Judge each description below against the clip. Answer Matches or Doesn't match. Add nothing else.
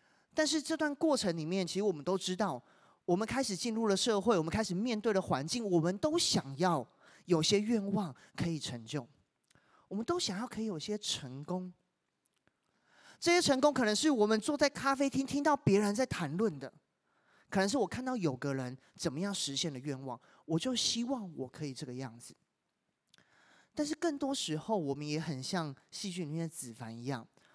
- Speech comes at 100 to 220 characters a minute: Doesn't match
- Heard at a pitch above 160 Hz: Matches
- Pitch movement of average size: Doesn't match